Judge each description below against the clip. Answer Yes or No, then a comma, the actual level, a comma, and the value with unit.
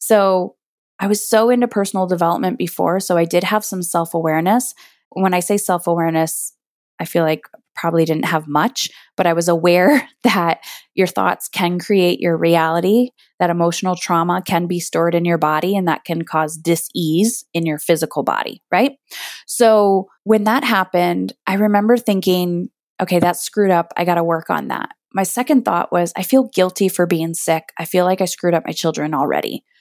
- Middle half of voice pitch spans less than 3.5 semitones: Yes, average, 3.1 semitones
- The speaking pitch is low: No, medium, 175 Hz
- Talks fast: No, average, 190 wpm